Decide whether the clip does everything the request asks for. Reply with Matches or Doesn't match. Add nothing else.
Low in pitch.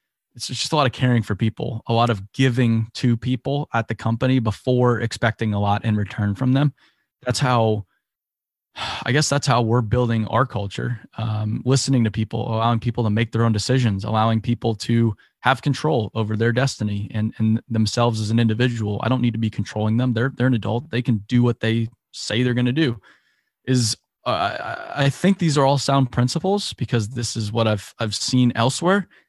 Matches